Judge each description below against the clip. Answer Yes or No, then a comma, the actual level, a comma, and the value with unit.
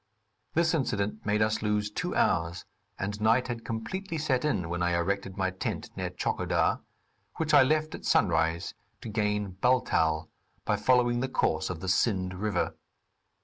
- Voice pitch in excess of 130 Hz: No, low, 105 Hz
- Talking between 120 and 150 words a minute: No, average, 160 wpm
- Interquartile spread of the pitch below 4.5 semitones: No, average, 5.1 semitones